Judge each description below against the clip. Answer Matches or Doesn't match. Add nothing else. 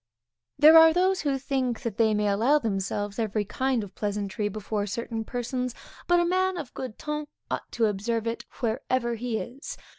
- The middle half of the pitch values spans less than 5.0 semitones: Matches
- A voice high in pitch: Matches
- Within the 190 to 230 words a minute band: Doesn't match